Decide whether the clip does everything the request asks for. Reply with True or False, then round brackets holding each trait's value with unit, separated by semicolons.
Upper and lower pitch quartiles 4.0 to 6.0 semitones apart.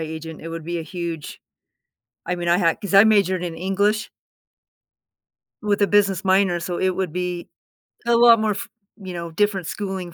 False (2.9 semitones)